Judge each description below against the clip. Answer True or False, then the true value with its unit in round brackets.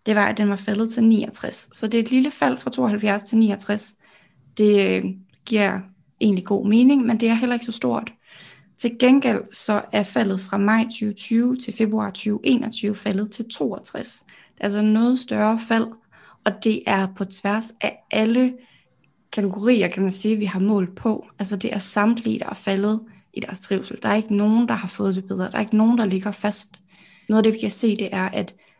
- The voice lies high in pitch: True (210 Hz)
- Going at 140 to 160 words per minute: False (210 wpm)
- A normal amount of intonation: False (2.1 semitones)